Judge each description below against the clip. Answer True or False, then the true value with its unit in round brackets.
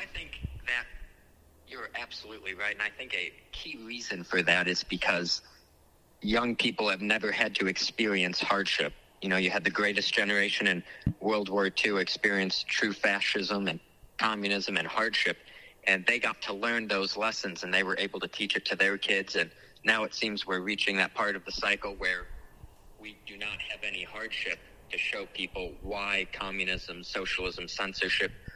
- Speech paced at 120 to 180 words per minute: True (175 wpm)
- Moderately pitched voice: False (100 Hz)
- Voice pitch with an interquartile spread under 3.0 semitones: True (2.6 semitones)